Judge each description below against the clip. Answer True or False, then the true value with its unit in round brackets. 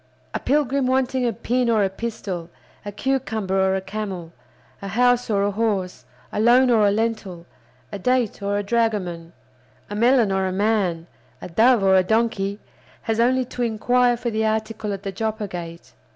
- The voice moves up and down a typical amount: True (3.7 semitones)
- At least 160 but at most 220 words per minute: True (180 wpm)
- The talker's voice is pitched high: True (215 Hz)